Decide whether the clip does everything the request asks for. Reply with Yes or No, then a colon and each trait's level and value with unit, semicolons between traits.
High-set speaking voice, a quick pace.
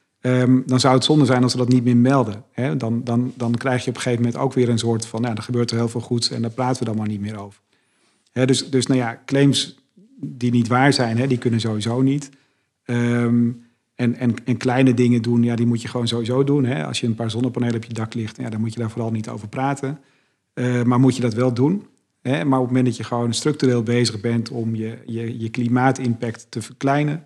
No: low, 120 Hz; fast, 255 wpm